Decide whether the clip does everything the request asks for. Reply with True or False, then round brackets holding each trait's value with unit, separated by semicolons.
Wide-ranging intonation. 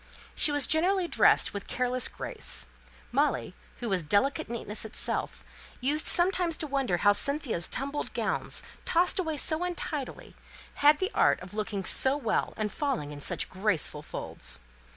True (7.2 semitones)